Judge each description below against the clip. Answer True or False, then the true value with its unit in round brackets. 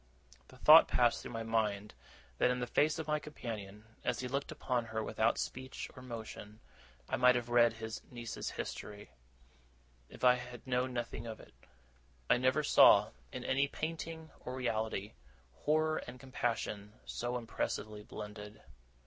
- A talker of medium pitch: False (120 Hz)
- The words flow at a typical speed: True (155 wpm)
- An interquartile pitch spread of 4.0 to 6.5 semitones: False (2.7 semitones)